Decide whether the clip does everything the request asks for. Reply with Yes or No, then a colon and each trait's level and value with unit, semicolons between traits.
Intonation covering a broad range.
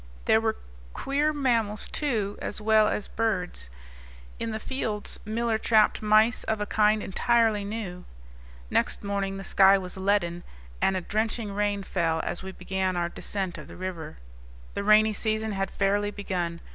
No: narrow, 2.4 semitones